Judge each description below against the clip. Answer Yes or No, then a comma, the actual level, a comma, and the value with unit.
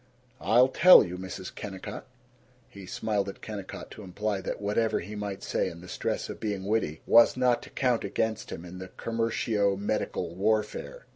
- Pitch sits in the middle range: No, low, 105 Hz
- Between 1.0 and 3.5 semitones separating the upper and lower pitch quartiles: Yes, average, 2.9 semitones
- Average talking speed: Yes, average, 175 wpm